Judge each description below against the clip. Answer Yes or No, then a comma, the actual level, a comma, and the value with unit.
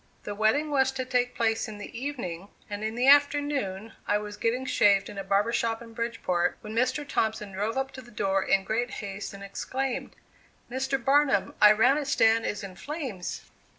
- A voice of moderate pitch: No, high, 225 Hz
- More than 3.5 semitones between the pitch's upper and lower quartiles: Yes, average, 4.4 semitones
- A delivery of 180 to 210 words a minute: Yes, average, 185 wpm